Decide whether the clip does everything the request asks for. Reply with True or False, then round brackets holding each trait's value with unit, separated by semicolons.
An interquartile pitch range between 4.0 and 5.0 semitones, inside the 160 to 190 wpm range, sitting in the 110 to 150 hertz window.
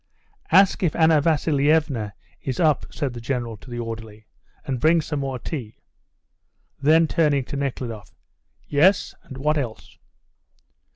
False (4.6 semitones; 135 wpm; 140 Hz)